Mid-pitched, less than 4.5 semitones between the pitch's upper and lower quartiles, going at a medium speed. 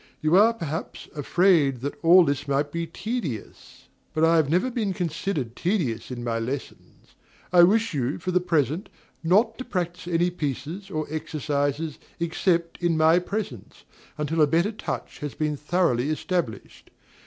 Yes: medium, 165 Hz; average, 3.9 semitones; average, 155 wpm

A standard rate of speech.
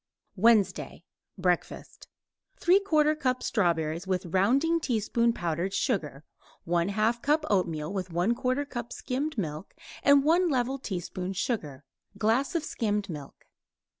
No: slow, 115 wpm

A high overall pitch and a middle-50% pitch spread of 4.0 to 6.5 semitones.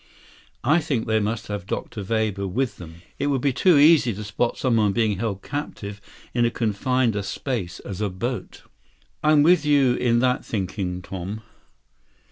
No: low, 110 Hz; average, 4.7 semitones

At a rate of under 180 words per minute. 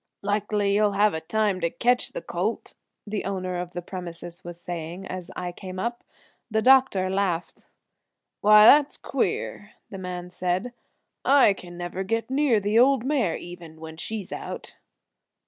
Yes: average, 165 wpm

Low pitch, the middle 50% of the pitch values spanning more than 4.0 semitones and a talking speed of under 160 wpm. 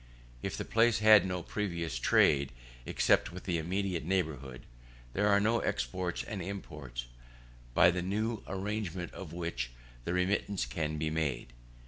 Yes: very low, 90 Hz; average, 4.5 semitones; average, 145 wpm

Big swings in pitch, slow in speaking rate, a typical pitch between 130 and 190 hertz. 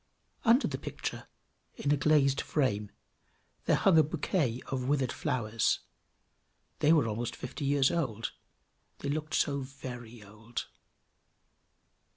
No: average, 3.9 semitones; slow, 125 wpm; low, 135 Hz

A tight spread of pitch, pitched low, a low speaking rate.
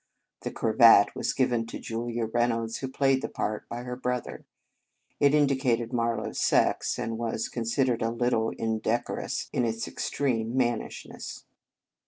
No: narrow, 1.7 semitones; low, 120 Hz; average, 150 wpm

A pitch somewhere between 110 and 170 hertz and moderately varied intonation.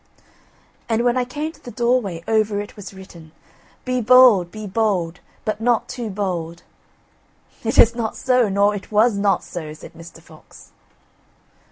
No: high, 210 Hz; average, 4.4 semitones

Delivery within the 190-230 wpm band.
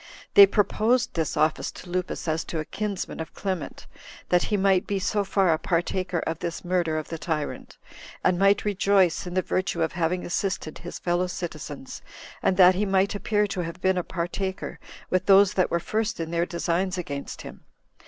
Yes: average, 195 wpm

